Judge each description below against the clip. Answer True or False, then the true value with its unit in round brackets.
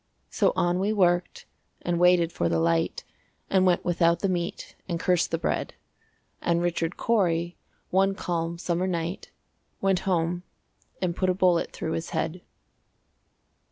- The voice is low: False (175 Hz)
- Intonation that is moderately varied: False (1.5 semitones)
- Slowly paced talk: False (150 wpm)